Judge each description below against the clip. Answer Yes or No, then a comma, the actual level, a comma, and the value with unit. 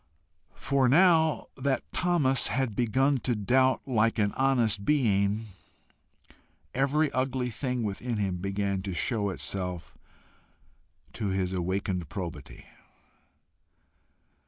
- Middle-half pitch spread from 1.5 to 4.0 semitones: No, average, 5.2 semitones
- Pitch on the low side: Yes, low, 115 Hz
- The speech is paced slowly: Yes, slow, 105 wpm